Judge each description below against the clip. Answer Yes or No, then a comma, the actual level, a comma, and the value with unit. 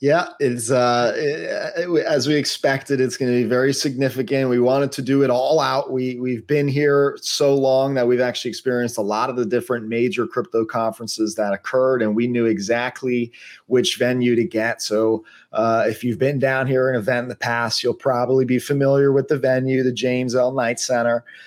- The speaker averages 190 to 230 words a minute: Yes, average, 200 wpm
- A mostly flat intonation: Yes, narrow, 2.1 semitones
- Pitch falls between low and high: No, low, 125 Hz